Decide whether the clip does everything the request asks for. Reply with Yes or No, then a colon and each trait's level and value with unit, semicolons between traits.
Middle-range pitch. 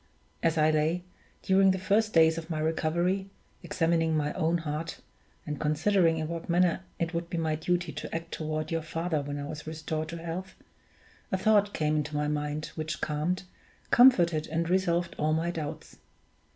Yes: medium, 165 Hz